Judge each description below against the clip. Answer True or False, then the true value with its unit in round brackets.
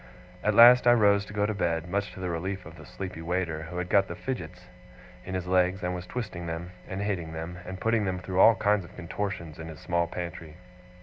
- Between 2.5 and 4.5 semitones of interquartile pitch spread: True (3.1 semitones)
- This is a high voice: False (90 Hz)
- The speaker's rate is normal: False (235 wpm)